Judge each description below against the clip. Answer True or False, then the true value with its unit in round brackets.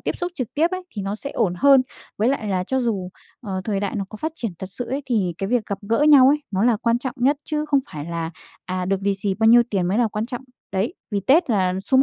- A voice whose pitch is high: True (225 Hz)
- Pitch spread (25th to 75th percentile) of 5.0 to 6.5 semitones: True (5.3 semitones)